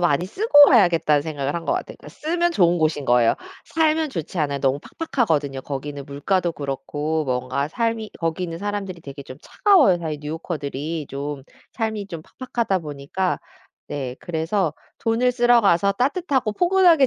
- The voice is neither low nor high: Yes, medium, 170 Hz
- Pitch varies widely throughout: Yes, wide, 8.0 semitones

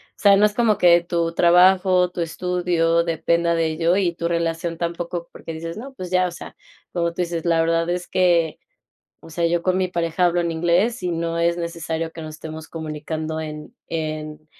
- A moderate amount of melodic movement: No, narrow, 1.4 semitones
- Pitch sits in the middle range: Yes, medium, 170 Hz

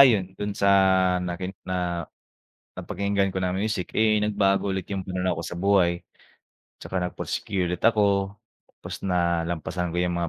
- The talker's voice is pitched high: No, very low, 95 Hz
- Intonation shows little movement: Yes, narrow, 2.1 semitones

